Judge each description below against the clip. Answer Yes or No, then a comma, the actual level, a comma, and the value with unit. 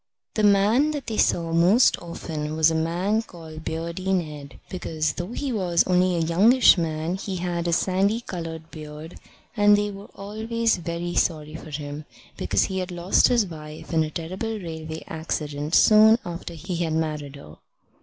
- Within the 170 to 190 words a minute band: Yes, average, 175 wpm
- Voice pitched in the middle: Yes, medium, 170 Hz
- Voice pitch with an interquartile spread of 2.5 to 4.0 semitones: Yes, average, 3.7 semitones